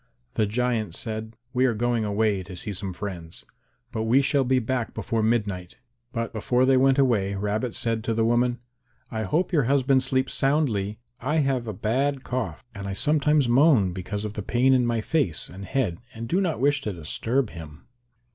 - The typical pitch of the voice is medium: No, low, 115 Hz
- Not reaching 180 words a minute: No, average, 195 wpm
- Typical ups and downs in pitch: Yes, average, 4.1 semitones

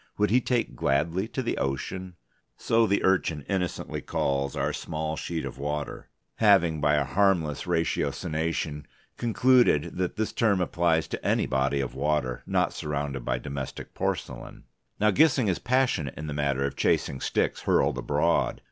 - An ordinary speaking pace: Yes, average, 155 wpm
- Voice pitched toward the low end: Yes, very low, 80 Hz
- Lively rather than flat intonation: Yes, wide, 5.8 semitones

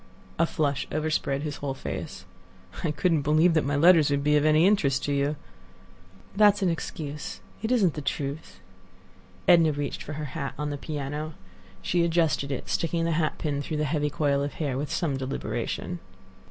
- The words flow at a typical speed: Yes, average, 185 wpm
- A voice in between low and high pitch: Yes, medium, 150 Hz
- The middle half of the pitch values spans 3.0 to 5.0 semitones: No, narrow, 2.5 semitones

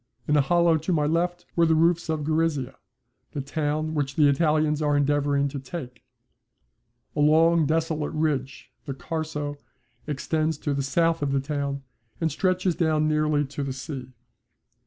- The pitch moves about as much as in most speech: No, narrow, 2.2 semitones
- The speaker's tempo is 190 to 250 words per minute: No, average, 160 wpm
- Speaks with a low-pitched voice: No, medium, 150 Hz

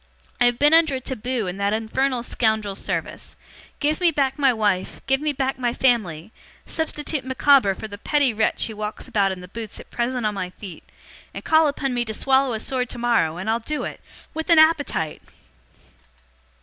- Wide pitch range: No, average, 4.6 semitones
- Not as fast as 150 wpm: No, average, 195 wpm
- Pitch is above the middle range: Yes, high, 245 Hz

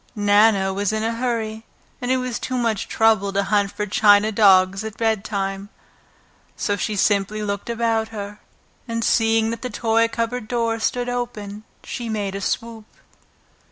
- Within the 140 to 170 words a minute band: Yes, average, 160 wpm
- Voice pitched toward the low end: No, high, 220 Hz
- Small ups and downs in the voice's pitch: Yes, narrow, 2.1 semitones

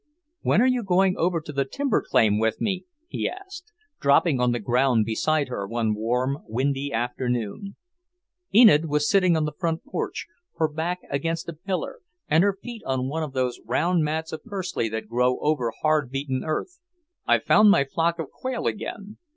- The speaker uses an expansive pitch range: Yes, wide, 6.4 semitones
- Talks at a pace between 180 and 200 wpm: Yes, average, 185 wpm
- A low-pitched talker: No, medium, 150 Hz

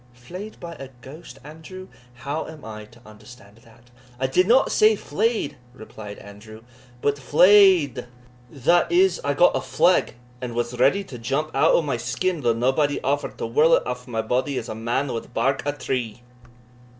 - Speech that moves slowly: No, average, 180 wpm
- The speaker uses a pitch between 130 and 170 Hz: Yes, low, 135 Hz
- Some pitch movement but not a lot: No, wide, 5.7 semitones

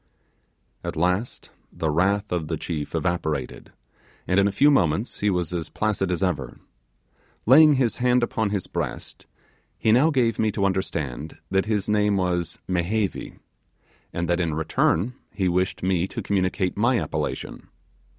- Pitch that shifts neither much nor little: Yes, average, 3.7 semitones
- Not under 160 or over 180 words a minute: No, average, 150 wpm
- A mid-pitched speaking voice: No, very low, 95 Hz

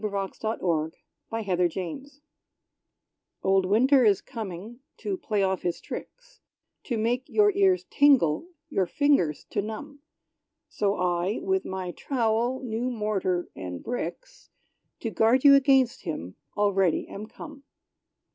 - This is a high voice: Yes, high, 220 Hz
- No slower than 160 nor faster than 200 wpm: No, slow, 135 wpm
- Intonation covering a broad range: Yes, wide, 6.3 semitones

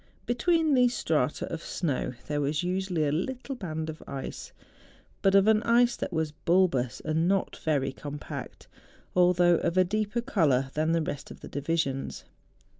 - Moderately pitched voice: Yes, medium, 170 Hz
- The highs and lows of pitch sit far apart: No, average, 5.0 semitones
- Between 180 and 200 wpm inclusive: No, average, 165 wpm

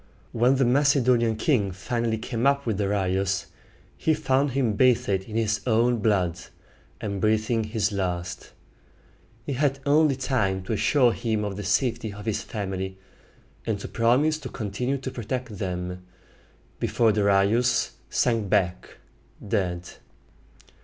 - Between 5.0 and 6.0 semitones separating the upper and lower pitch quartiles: No, average, 4.1 semitones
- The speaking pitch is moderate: No, low, 110 Hz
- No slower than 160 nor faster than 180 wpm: No, slow, 135 wpm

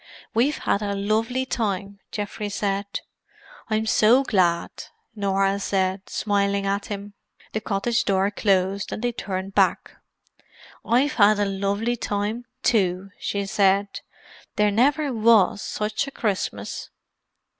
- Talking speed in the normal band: No, slow, 125 wpm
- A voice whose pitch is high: Yes, high, 205 Hz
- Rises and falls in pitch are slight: Yes, narrow, 2.0 semitones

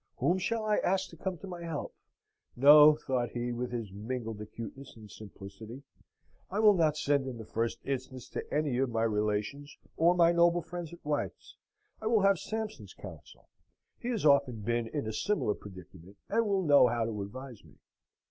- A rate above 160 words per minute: Yes, average, 185 wpm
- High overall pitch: No, low, 135 Hz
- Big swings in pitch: Yes, wide, 7.3 semitones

